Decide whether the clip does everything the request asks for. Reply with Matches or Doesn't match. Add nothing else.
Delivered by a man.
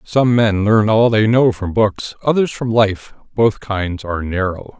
Matches